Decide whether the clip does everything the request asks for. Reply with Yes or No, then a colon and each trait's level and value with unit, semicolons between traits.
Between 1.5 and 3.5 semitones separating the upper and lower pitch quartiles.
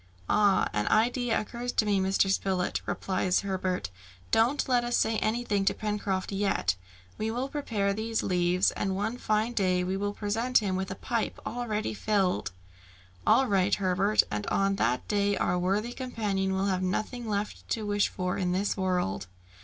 Yes: average, 2.8 semitones